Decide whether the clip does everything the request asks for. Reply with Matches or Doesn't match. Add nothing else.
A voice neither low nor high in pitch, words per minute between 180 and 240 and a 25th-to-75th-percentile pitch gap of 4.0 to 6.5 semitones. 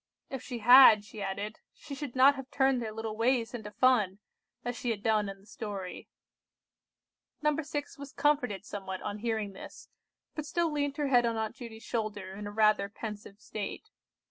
Doesn't match